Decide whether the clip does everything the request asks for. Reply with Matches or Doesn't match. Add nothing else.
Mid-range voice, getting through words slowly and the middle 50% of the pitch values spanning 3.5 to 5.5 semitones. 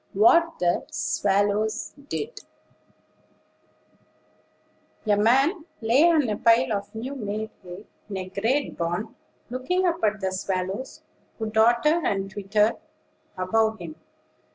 Doesn't match